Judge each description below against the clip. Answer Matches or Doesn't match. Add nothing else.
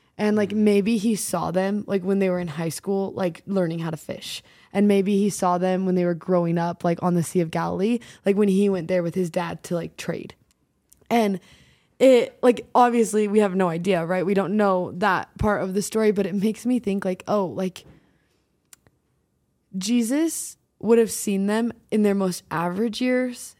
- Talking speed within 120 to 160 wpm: Doesn't match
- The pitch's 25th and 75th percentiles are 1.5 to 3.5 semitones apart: Matches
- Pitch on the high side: Matches